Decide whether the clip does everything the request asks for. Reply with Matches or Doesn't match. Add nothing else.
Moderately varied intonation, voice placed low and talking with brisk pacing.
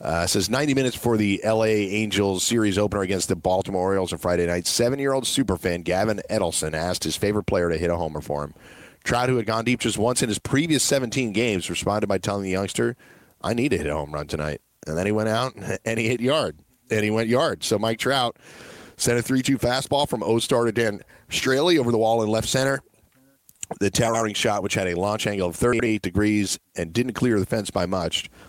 Matches